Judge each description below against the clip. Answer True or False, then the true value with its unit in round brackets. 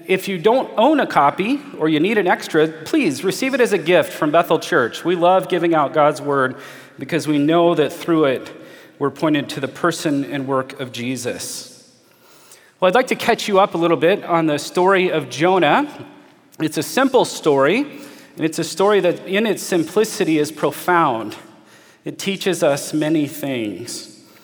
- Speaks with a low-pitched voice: False (170 Hz)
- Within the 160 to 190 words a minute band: True (185 wpm)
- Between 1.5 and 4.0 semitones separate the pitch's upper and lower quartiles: False (4.4 semitones)